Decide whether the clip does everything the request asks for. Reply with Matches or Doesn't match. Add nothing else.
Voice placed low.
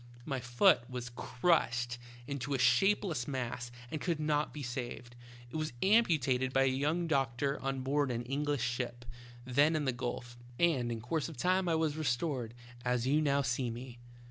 Matches